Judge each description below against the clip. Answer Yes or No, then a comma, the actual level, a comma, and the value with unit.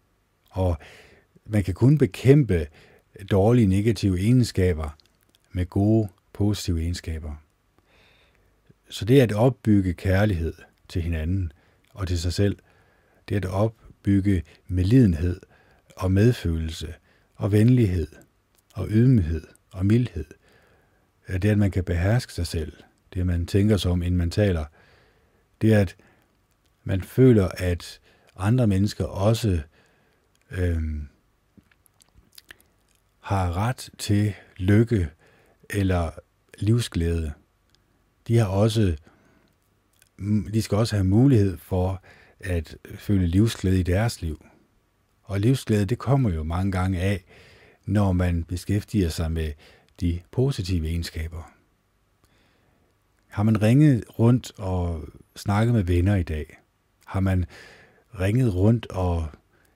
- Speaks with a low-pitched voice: Yes, very low, 95 Hz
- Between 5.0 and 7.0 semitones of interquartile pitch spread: No, average, 3.2 semitones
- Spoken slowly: Yes, slow, 110 wpm